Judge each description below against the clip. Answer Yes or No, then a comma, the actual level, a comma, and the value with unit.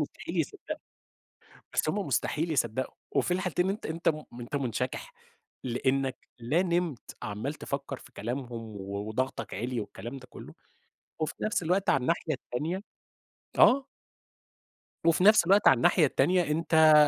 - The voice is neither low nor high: Yes, medium, 145 Hz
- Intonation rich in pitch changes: Yes, wide, 5.7 semitones